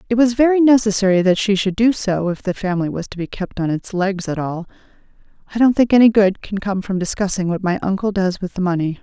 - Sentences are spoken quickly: Yes, fast, 245 wpm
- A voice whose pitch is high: Yes, high, 200 Hz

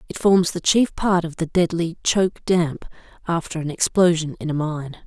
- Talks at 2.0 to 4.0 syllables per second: No, 4.8 syllables/s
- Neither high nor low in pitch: Yes, medium, 165 Hz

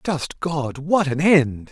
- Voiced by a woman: No, male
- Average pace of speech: Yes, average, 175 wpm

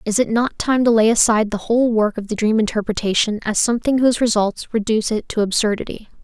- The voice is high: Yes, high, 220 Hz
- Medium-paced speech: No, fast, 210 wpm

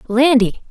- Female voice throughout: Yes, female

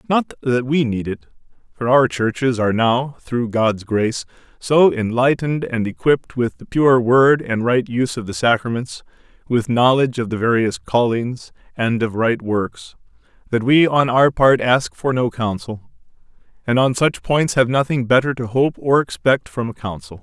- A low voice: Yes, low, 120 Hz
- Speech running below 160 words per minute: No, average, 180 wpm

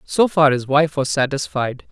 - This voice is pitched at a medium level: Yes, medium, 145 Hz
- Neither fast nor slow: Yes, average, 190 wpm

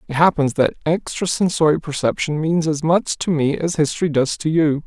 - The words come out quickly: No, average, 185 wpm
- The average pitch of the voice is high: No, medium, 155 Hz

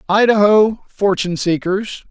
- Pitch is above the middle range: Yes, high, 195 Hz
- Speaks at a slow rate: Yes, slow, 85 wpm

